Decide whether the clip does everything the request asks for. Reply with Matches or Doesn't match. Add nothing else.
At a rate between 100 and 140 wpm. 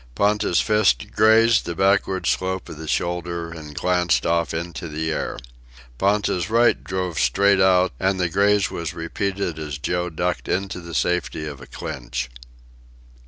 Doesn't match